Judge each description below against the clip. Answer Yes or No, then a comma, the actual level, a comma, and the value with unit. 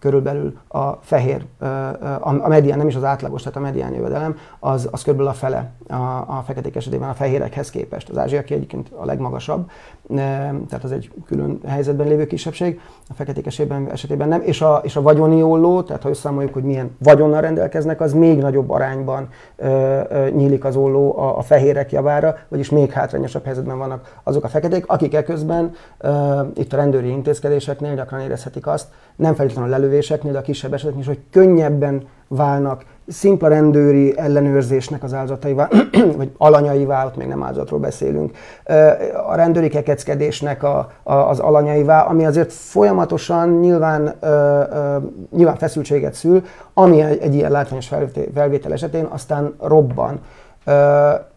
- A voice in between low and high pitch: Yes, medium, 145 Hz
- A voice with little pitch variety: Yes, narrow, 2.0 semitones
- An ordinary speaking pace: No, fast, 160 wpm